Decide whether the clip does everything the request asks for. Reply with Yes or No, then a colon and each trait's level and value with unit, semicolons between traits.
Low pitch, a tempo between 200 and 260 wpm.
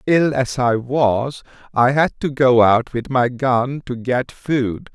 No: low, 130 Hz; average, 180 wpm